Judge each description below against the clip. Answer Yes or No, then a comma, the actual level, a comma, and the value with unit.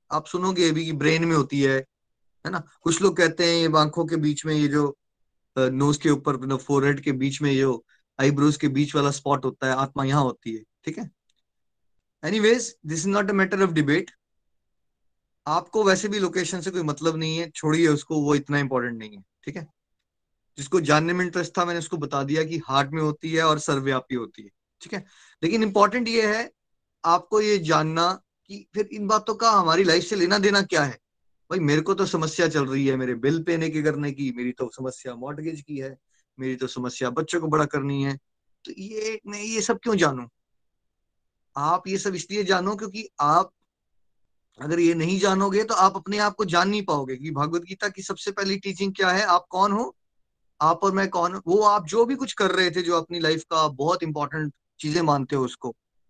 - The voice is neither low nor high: Yes, medium, 160 Hz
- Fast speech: Yes, fast, 205 wpm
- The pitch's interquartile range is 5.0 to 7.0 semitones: Yes, wide, 5.4 semitones